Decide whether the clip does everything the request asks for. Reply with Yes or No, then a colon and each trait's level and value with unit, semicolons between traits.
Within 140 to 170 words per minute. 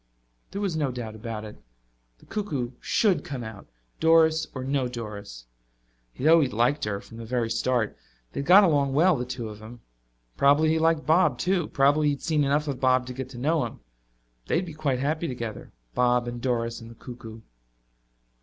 No: average, 200 wpm